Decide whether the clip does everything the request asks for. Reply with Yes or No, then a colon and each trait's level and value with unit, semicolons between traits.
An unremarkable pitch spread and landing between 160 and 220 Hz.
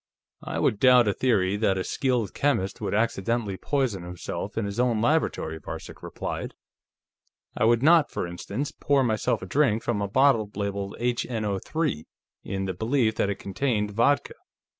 No: average, 4.5 semitones; low, 110 Hz